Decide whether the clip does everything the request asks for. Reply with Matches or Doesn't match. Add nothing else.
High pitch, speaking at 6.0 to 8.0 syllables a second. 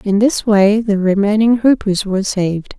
Doesn't match